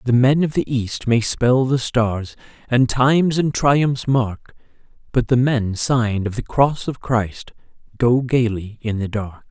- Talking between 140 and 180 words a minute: Yes, average, 175 wpm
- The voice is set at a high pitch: No, low, 120 Hz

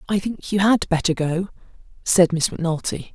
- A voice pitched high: No, medium, 180 Hz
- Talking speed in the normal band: Yes, average, 170 wpm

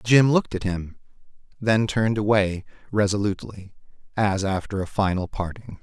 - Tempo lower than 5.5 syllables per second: Yes, 5.1 syllables/s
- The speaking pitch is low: Yes, low, 100 Hz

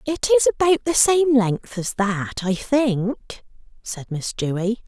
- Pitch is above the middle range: Yes, high, 235 Hz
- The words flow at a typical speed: Yes, average, 160 wpm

